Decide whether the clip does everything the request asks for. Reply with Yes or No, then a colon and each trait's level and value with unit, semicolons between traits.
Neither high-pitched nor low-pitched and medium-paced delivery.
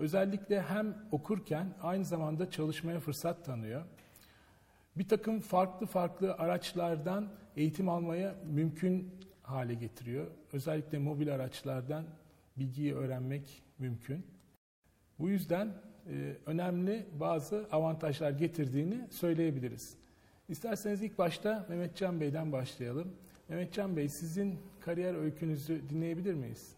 Yes: medium, 165 Hz; average, 105 wpm